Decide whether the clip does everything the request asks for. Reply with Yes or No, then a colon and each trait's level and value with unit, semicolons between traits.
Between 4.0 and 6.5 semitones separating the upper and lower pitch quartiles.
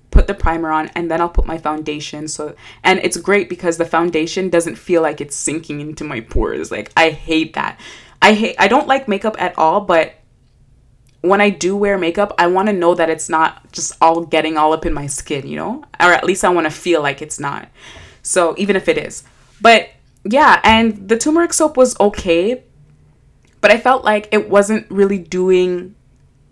Yes: average, 4.5 semitones